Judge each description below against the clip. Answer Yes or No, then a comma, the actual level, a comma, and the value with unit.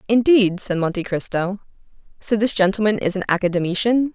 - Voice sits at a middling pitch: No, high, 200 Hz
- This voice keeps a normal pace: Yes, average, 145 wpm